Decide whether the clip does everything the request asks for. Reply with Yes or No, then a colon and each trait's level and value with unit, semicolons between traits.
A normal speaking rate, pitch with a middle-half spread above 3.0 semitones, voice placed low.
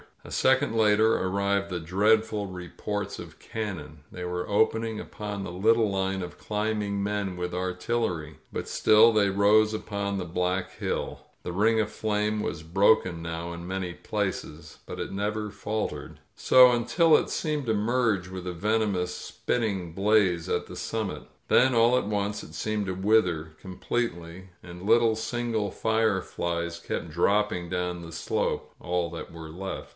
Yes: average, 165 wpm; average, 3.5 semitones; low, 100 Hz